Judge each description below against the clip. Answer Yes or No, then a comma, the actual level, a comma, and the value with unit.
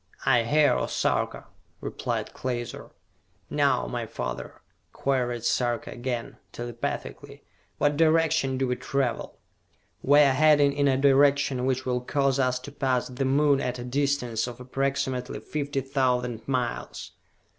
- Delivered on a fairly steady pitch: Yes, narrow, 2.3 semitones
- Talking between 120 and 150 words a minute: Yes, slow, 135 wpm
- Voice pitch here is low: Yes, low, 130 Hz